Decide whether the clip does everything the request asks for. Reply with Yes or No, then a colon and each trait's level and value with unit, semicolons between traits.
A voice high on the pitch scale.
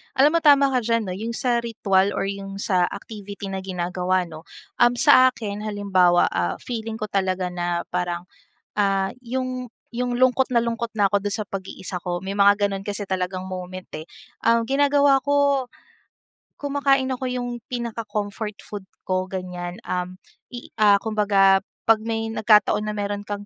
Yes: high, 205 Hz